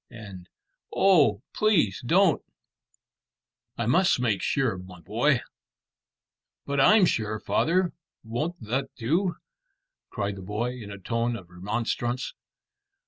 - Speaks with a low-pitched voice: Yes, low, 120 Hz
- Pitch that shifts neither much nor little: No, wide, 7.5 semitones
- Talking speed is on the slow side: Yes, slow, 115 wpm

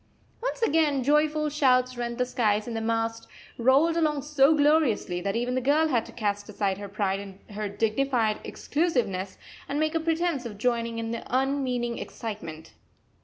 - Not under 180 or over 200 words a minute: No, average, 170 wpm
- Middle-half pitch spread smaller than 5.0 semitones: No, wide, 5.4 semitones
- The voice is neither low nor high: No, high, 245 Hz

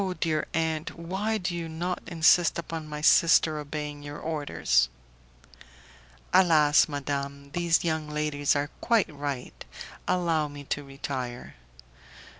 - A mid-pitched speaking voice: Yes, medium, 155 Hz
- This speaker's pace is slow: Yes, slow, 120 wpm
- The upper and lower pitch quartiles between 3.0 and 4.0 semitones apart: No, narrow, 2.6 semitones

